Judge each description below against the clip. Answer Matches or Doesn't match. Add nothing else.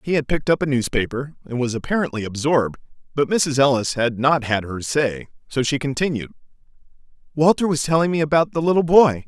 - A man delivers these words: Matches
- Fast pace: Doesn't match